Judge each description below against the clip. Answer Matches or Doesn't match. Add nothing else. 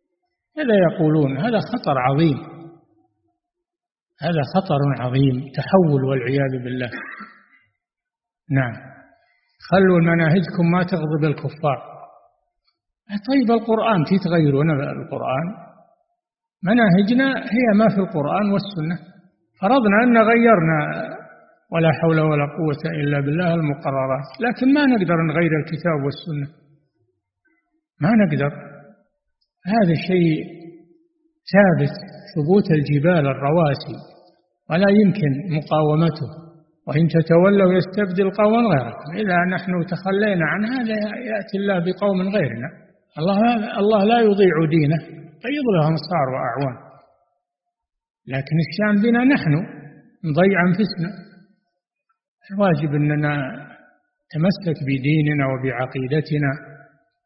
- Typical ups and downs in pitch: Doesn't match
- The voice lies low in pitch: Doesn't match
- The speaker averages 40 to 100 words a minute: Matches